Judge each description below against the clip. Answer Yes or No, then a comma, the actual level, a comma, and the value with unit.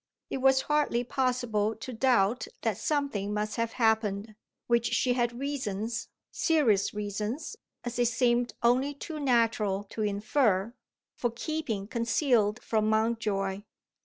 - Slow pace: Yes, slow, 130 wpm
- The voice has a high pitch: Yes, high, 230 Hz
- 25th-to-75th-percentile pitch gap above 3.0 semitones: Yes, average, 3.4 semitones